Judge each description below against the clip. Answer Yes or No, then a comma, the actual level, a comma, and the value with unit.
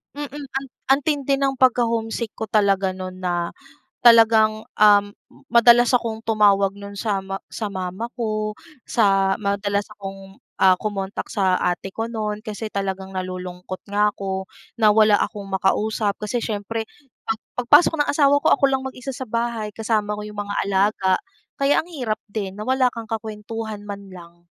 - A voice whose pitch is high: Yes, high, 210 Hz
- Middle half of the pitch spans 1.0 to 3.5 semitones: Yes, average, 2.8 semitones